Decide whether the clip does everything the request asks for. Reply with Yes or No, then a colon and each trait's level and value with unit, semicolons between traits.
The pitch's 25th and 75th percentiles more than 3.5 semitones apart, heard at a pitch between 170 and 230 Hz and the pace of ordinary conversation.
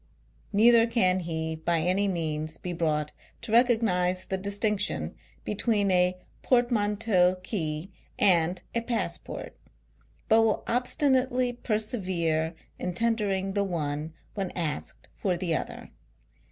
No: average, 4.8 semitones; high, 190 Hz; slow, 120 wpm